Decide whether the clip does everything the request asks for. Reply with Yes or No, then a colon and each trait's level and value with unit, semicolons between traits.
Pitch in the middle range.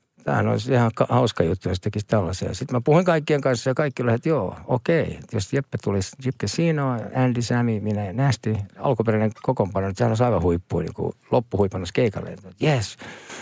No: low, 115 Hz